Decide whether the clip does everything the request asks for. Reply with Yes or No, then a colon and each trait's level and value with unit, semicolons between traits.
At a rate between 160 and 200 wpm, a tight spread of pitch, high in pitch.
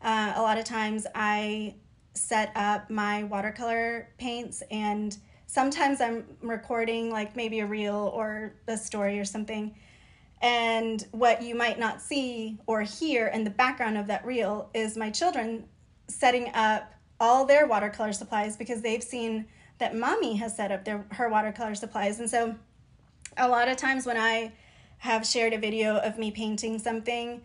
Yes: average, 165 wpm; narrow, 1.7 semitones; high, 225 Hz